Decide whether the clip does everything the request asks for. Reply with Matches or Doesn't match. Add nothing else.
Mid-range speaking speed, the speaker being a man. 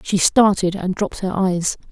Doesn't match